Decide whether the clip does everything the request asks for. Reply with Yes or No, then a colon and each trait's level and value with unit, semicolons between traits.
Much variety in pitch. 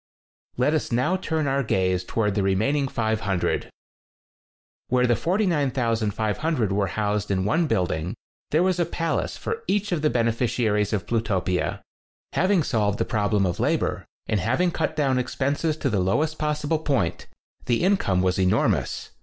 Yes: wide, 7.0 semitones